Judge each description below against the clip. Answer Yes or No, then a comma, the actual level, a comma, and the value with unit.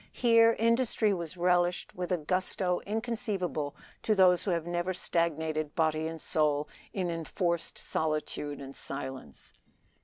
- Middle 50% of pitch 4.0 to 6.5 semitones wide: No, average, 3.3 semitones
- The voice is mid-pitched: Yes, medium, 175 Hz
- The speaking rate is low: Yes, slow, 130 wpm